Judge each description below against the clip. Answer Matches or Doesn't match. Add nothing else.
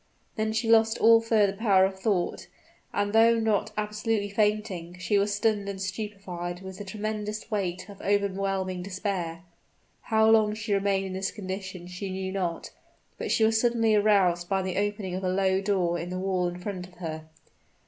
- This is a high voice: Matches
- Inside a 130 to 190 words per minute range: Matches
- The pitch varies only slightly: Matches